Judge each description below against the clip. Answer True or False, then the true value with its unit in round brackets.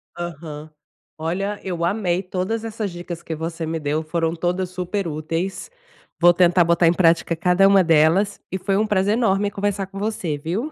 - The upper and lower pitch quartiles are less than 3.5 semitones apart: True (3.0 semitones)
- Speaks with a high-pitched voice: False (180 Hz)